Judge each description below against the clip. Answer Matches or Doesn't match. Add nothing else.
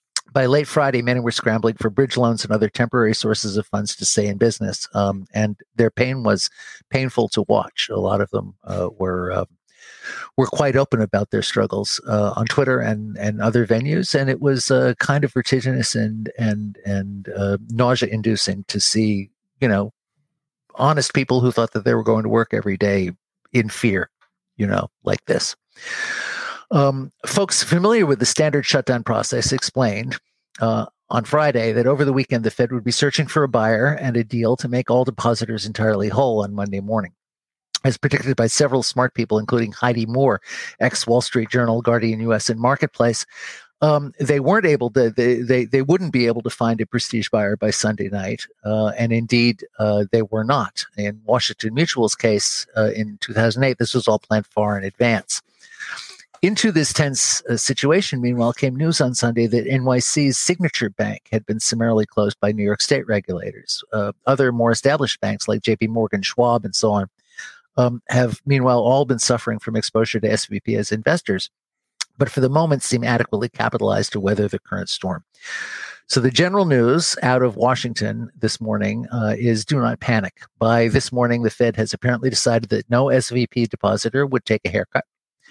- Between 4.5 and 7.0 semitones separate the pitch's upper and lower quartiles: Doesn't match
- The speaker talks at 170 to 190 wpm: Matches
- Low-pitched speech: Matches